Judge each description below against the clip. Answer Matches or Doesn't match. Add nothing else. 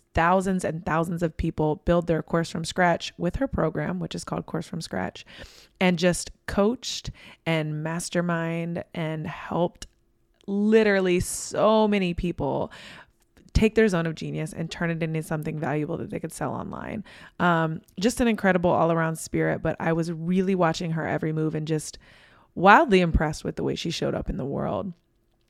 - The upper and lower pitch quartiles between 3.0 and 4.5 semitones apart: Doesn't match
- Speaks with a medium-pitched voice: Matches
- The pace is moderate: Matches